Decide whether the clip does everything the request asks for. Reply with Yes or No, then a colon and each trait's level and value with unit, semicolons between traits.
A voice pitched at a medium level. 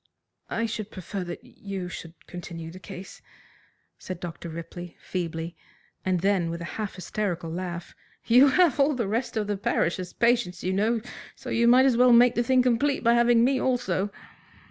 No: high, 200 Hz